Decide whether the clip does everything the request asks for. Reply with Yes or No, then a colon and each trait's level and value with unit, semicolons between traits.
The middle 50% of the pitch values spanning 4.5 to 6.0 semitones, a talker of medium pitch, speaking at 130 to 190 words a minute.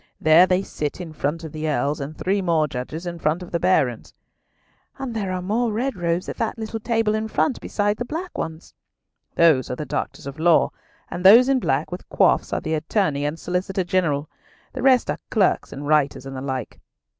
No: wide, 5.4 semitones; medium, 175 Hz; fast, 205 wpm